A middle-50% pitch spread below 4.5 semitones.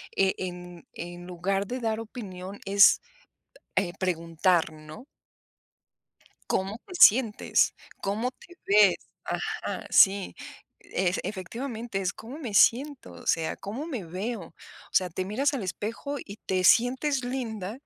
No: average, 5.0 semitones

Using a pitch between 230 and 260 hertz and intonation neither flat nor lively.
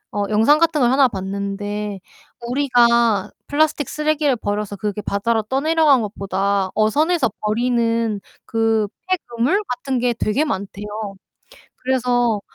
Yes: high, 235 Hz; average, 4.6 semitones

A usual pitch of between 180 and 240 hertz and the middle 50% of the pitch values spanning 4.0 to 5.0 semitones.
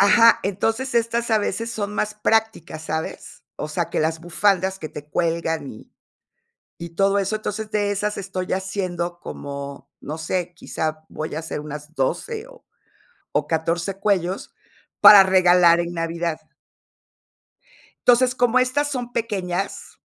Yes: medium, 185 Hz; average, 4.4 semitones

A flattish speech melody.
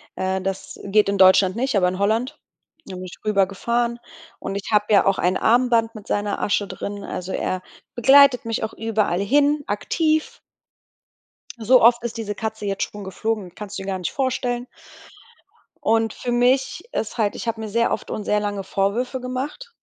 No: average, 3.5 semitones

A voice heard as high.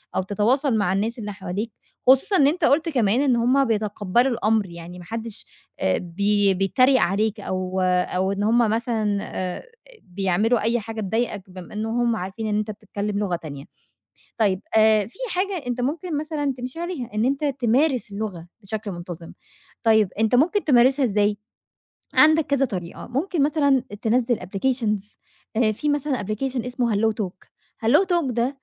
Yes: high, 225 Hz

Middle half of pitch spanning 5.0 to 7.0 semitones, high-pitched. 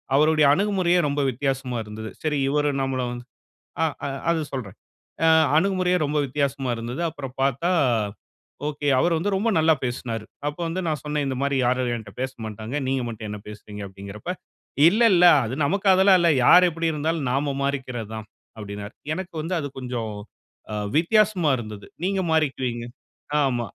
No: wide, 5.4 semitones; medium, 140 Hz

